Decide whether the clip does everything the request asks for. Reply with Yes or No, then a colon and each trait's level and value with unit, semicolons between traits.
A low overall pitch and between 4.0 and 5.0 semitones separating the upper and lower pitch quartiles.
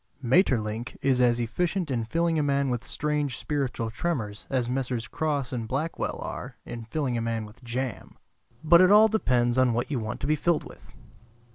Yes: low, 130 Hz; average, 4.4 semitones